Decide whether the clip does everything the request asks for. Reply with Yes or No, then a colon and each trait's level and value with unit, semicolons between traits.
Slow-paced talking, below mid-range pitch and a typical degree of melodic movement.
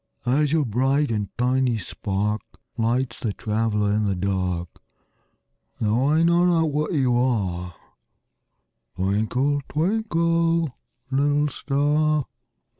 No: slow, 110 wpm; low, 130 Hz; wide, 6.1 semitones